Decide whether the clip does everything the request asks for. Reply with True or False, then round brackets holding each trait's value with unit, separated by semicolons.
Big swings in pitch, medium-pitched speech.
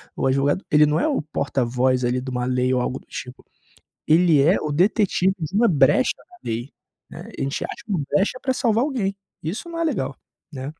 True (7.6 semitones; 150 Hz)